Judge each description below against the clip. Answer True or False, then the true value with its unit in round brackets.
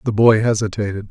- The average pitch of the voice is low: True (105 Hz)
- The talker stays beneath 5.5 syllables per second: False (6.1 syllables/s)